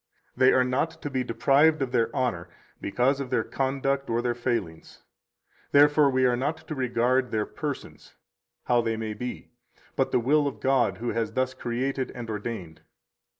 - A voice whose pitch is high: No, low, 125 Hz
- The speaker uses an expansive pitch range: No, average, 2.8 semitones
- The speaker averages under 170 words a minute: No, average, 175 wpm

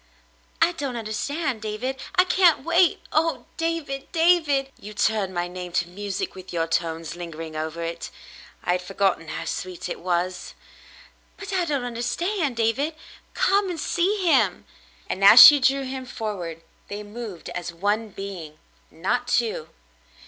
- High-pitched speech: Yes, high, 220 Hz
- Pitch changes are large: Yes, wide, 8.4 semitones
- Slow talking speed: No, average, 155 wpm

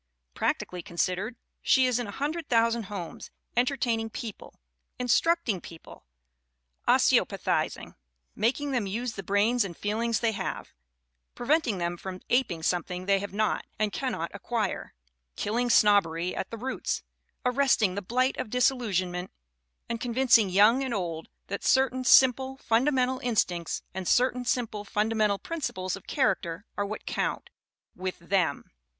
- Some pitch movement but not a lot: Yes, average, 4.7 semitones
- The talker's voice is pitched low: No, high, 220 Hz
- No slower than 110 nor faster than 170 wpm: Yes, average, 145 wpm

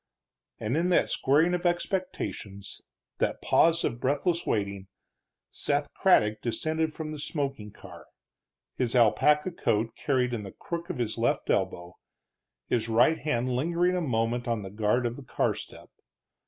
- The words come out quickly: No, average, 155 wpm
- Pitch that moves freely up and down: Yes, wide, 6.3 semitones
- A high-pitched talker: No, low, 125 Hz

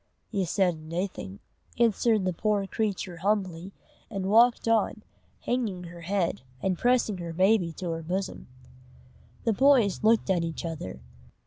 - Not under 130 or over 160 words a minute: Yes, average, 140 wpm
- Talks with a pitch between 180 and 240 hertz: Yes, high, 190 Hz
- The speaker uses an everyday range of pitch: Yes, average, 4.1 semitones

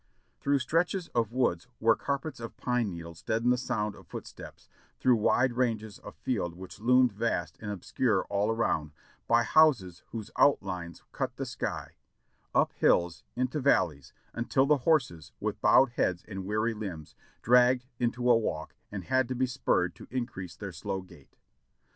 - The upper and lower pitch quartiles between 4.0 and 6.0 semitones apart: Yes, average, 5.1 semitones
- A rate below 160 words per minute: No, average, 165 wpm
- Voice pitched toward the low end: Yes, low, 115 Hz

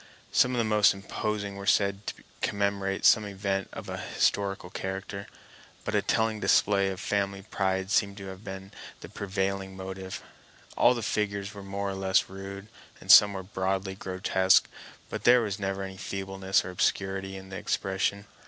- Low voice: Yes, very low, 95 Hz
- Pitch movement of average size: No, narrow, 0.9 semitones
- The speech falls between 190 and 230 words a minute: No, average, 170 wpm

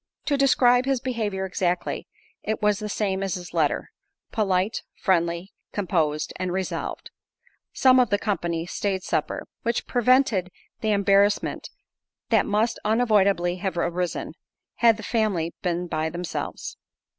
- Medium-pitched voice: No, high, 200 Hz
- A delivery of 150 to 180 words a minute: No, slow, 135 wpm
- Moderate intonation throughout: Yes, average, 3.8 semitones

